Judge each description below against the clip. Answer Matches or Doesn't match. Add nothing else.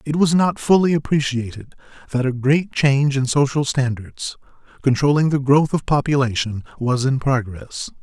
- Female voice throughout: Doesn't match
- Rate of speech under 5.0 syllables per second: Matches